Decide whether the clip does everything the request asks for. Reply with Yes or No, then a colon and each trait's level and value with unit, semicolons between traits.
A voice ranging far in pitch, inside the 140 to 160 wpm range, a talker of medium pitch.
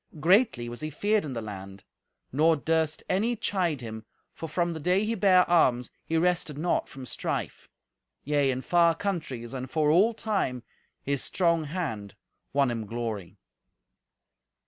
Yes: wide, 6.2 semitones; average, 155 wpm; medium, 155 Hz